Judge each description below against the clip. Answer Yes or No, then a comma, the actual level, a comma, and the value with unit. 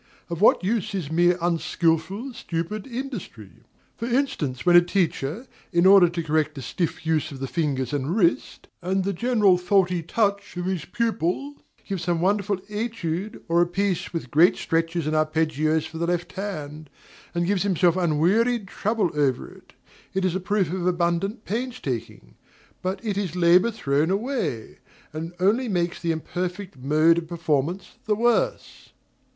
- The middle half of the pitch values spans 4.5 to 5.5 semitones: No, average, 3.9 semitones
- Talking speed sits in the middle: Yes, average, 160 wpm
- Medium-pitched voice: Yes, medium, 175 Hz